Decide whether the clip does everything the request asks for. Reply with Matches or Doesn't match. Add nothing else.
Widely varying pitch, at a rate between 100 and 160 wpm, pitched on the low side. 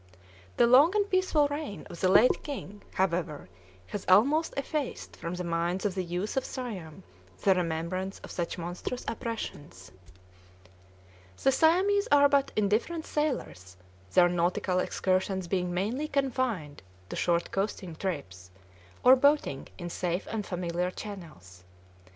Doesn't match